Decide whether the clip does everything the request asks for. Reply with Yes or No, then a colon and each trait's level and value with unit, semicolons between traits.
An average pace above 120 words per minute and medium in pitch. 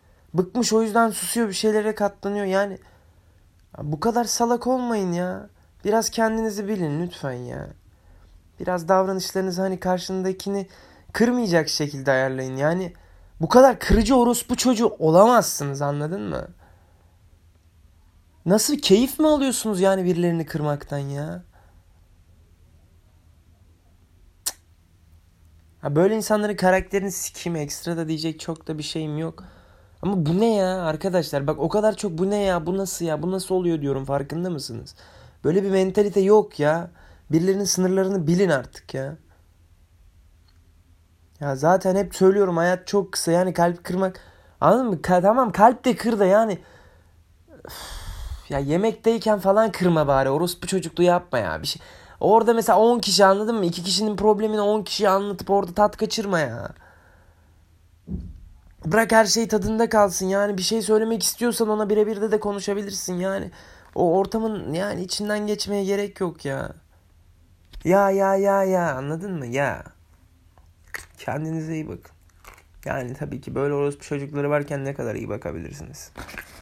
Yes: fast, 140 wpm; medium, 175 Hz